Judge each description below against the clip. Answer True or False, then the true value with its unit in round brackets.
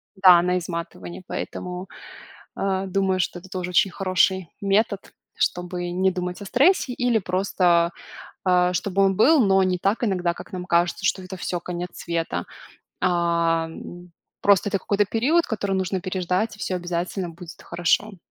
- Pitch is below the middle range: False (185 Hz)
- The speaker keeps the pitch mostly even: True (1.8 semitones)